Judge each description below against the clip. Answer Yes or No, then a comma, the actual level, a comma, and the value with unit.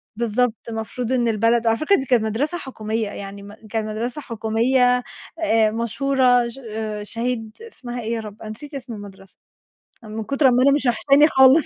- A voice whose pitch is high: Yes, high, 235 Hz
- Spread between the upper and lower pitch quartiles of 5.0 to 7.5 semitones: No, average, 3.1 semitones